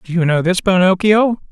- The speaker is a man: Yes, male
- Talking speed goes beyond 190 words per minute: Yes, average, 200 wpm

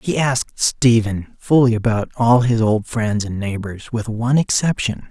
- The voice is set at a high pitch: No, low, 115 Hz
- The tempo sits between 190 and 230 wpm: No, average, 165 wpm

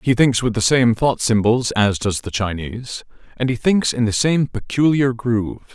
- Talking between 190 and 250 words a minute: Yes, average, 200 wpm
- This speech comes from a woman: No, male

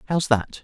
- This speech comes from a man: Yes, male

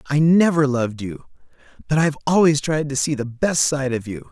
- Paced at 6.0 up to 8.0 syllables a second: No, 5.4 syllables/s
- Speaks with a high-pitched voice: No, medium, 140 Hz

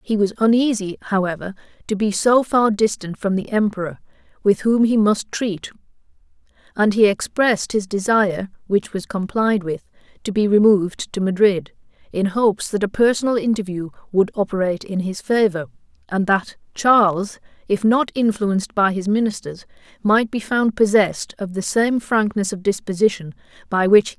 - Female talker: Yes, female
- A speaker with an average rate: Yes, average, 165 wpm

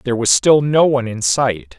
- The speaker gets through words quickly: Yes, fast, 235 wpm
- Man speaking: Yes, male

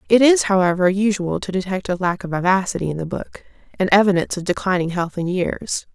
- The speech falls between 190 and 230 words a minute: Yes, average, 200 wpm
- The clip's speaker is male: No, female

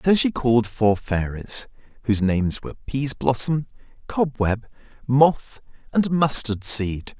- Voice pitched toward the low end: Yes, low, 125 Hz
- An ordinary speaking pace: No, slow, 110 wpm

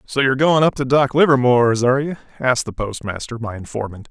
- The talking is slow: No, fast, 205 wpm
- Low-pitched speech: Yes, low, 125 Hz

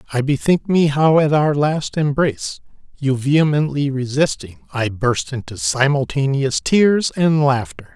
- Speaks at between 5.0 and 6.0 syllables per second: No, 4.3 syllables/s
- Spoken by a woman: No, male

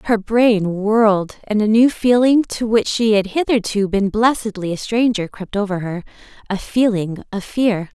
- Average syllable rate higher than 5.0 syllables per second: No, 4.5 syllables/s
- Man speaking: No, female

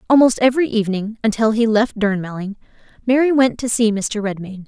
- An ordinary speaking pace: Yes, average, 165 wpm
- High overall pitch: Yes, high, 220 Hz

